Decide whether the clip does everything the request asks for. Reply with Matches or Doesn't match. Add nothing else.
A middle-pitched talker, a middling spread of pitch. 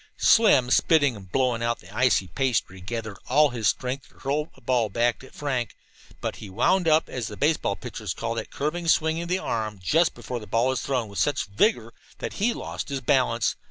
Doesn't match